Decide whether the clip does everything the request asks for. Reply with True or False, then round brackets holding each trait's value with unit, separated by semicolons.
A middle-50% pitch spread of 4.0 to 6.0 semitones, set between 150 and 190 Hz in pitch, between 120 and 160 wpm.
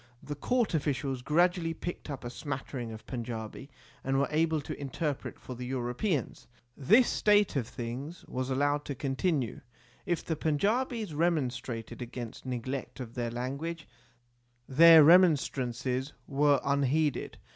False (4.3 semitones; 140 Hz; 135 wpm)